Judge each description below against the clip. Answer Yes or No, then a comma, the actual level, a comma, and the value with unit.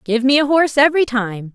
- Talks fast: Yes, fast, 235 wpm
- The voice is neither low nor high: No, very high, 260 Hz